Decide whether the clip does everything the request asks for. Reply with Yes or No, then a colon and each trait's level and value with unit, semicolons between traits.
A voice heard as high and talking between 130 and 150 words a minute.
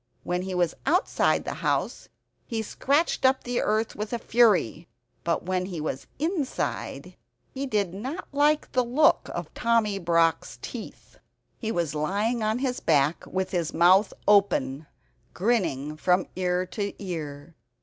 Yes: high, 195 Hz; average, 145 wpm